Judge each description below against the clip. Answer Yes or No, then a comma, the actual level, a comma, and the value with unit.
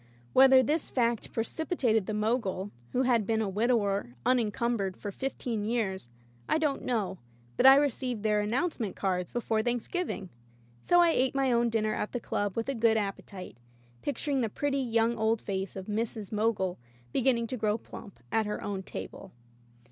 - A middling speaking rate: Yes, average, 185 wpm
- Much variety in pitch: No, average, 3.6 semitones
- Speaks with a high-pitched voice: Yes, high, 225 Hz